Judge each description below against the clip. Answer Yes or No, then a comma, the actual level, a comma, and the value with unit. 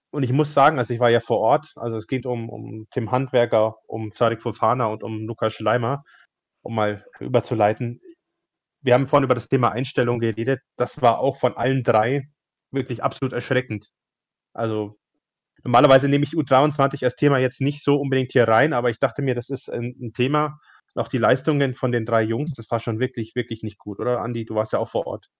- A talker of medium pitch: No, low, 125 Hz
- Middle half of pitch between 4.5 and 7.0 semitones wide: No, average, 3.0 semitones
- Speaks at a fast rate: Yes, fast, 205 wpm